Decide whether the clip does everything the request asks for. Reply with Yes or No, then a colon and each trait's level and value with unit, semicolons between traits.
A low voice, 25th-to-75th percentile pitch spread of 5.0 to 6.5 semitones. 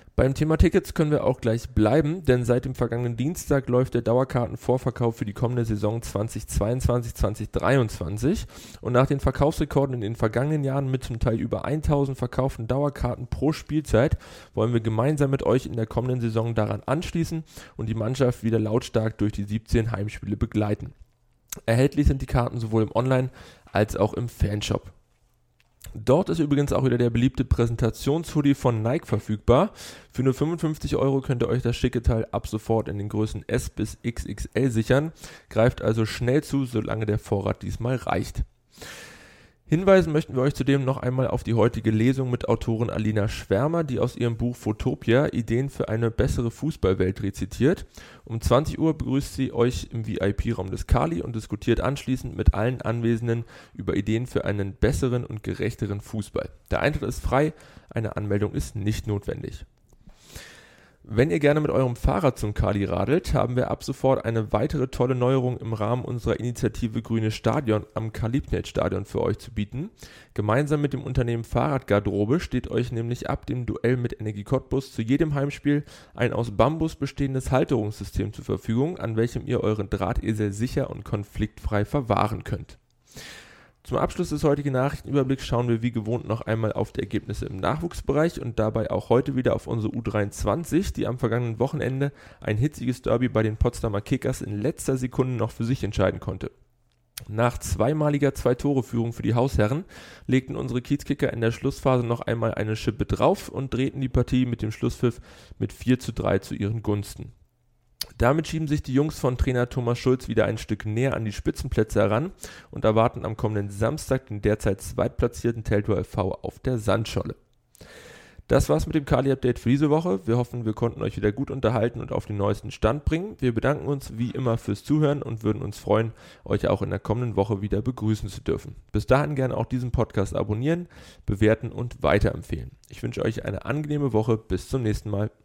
No: low, 120 Hz; average, 3.6 semitones